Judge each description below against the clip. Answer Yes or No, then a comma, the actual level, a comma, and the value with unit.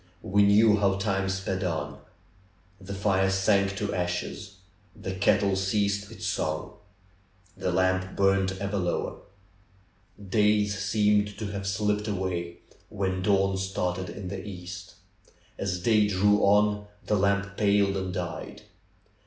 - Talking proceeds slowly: Yes, slow, 130 wpm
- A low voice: Yes, low, 100 Hz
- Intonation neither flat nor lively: No, narrow, 1.6 semitones